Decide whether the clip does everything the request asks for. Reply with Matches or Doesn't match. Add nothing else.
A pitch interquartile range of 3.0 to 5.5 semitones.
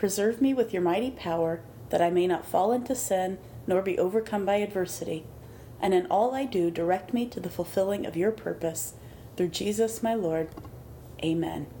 Matches